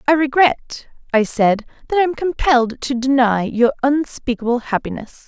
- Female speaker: Yes, female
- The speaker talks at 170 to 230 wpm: No, average, 150 wpm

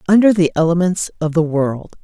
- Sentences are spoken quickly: No, average, 175 wpm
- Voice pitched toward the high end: No, medium, 170 Hz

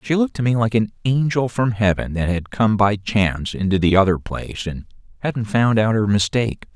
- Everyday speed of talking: No, fast, 215 wpm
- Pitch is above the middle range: No, low, 105 Hz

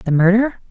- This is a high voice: Yes, high, 205 Hz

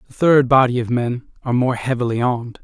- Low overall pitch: Yes, low, 125 Hz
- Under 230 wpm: Yes, fast, 205 wpm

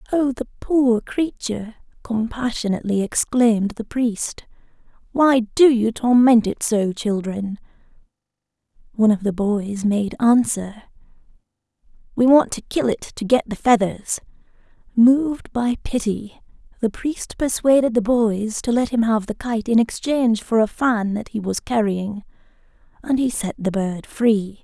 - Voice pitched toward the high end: Yes, high, 230 Hz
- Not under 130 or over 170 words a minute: Yes, average, 140 wpm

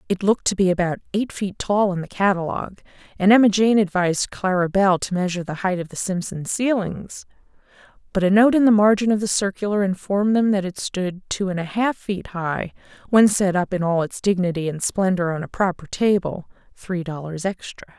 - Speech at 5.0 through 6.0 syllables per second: Yes, 5.6 syllables/s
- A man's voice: No, female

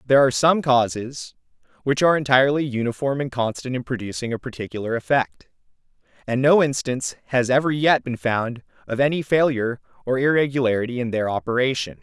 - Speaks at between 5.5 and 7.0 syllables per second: Yes, 6.1 syllables/s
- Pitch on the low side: Yes, low, 125 Hz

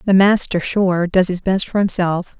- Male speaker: No, female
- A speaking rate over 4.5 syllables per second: No, 4.4 syllables/s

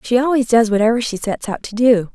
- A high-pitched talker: Yes, high, 230 Hz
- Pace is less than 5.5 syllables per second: No, 5.9 syllables/s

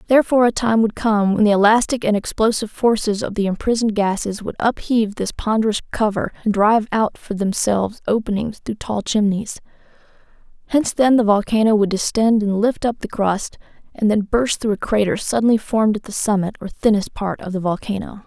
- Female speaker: Yes, female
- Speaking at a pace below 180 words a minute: No, average, 185 wpm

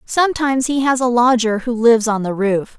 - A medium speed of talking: No, fast, 215 wpm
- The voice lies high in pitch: Yes, high, 240 Hz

